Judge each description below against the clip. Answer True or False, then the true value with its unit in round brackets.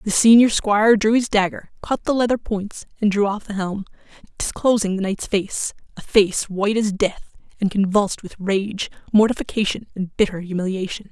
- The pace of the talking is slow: False (165 wpm)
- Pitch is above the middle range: True (205 Hz)